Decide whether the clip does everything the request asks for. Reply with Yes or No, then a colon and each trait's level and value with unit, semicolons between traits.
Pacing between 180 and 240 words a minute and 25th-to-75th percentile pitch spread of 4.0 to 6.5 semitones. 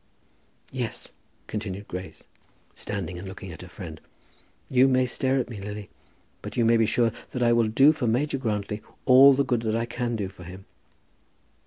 Yes: average, 185 wpm; average, 4.3 semitones